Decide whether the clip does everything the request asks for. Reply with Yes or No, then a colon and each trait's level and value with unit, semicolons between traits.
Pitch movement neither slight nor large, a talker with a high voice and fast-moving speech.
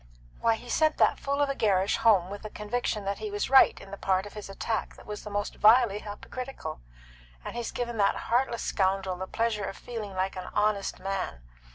Yes: average, 3.5 semitones; high, 210 Hz; fast, 215 wpm